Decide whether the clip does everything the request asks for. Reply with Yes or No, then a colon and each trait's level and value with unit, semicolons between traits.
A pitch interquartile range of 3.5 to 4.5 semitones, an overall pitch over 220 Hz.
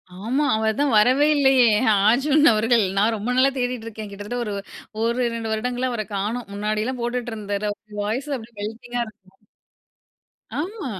No: average, 2.7 semitones; high, 230 Hz